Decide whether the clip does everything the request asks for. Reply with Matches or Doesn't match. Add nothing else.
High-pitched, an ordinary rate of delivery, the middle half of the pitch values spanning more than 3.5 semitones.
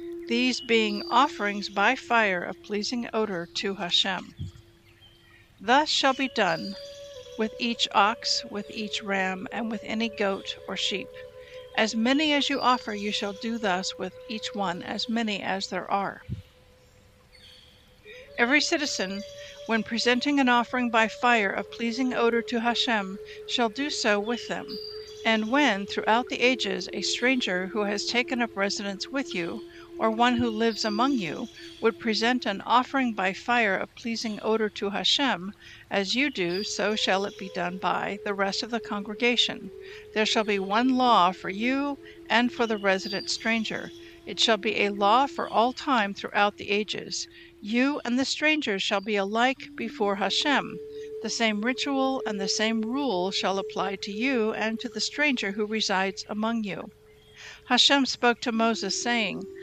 Matches